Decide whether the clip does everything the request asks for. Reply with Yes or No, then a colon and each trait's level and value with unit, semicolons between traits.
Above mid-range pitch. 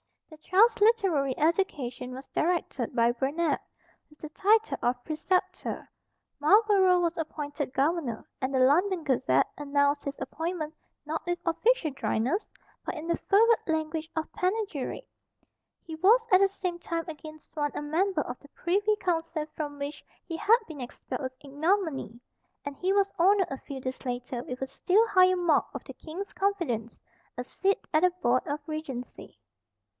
Yes: very high, 315 Hz